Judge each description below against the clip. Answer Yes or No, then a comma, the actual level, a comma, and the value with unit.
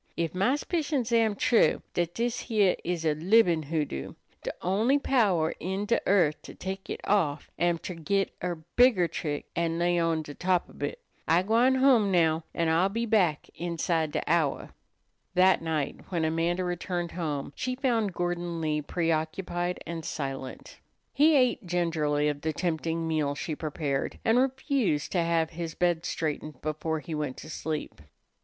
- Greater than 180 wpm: No, average, 170 wpm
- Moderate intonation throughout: Yes, average, 3.9 semitones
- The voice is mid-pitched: Yes, medium, 170 Hz